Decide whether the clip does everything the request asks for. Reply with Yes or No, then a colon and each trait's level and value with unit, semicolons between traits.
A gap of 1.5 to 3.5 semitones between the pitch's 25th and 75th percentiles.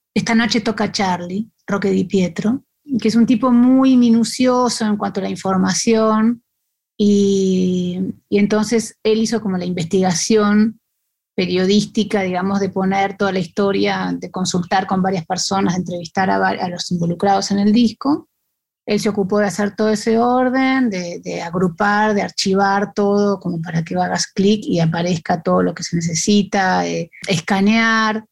Yes: average, 2.9 semitones